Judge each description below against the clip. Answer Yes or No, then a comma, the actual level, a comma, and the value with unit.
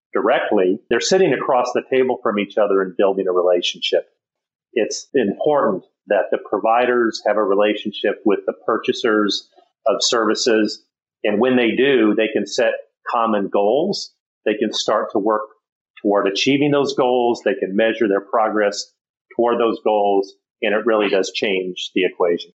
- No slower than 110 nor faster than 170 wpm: Yes, average, 155 wpm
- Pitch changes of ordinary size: Yes, average, 3.0 semitones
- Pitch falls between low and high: No, low, 105 Hz